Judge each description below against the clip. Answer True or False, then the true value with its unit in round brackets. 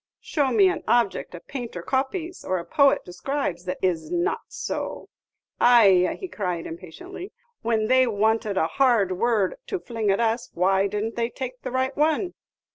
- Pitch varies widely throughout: True (5.8 semitones)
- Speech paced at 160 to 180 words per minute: True (170 wpm)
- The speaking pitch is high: True (230 Hz)